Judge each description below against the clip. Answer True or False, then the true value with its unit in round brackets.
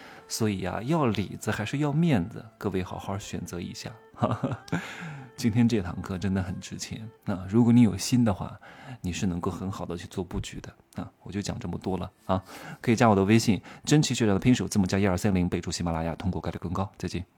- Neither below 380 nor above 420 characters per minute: False (325 characters per minute)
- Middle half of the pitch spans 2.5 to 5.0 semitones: True (4.3 semitones)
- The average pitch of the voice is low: True (100 Hz)